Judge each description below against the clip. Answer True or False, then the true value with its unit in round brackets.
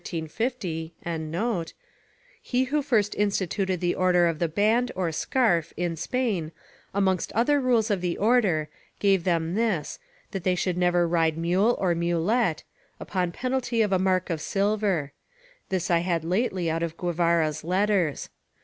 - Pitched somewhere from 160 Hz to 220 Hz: True (185 Hz)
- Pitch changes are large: False (3.8 semitones)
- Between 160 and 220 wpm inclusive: False (150 wpm)